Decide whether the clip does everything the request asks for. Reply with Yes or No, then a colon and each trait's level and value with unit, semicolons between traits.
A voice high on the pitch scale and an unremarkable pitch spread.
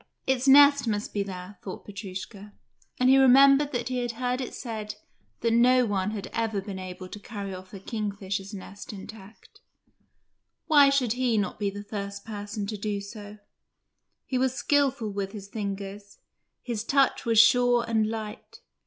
Yes: high, 215 Hz; average, 3.7 semitones